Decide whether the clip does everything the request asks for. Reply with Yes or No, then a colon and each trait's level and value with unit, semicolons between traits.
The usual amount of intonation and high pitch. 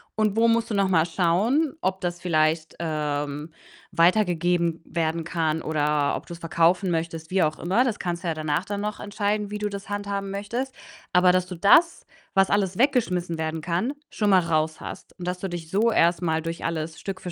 No: average, 3.7 semitones; medium, 175 Hz